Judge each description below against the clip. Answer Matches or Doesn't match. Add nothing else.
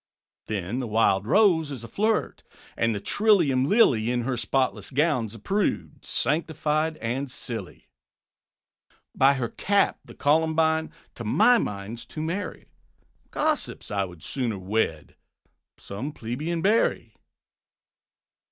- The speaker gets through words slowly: Matches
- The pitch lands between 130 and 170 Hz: Matches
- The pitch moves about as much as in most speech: Doesn't match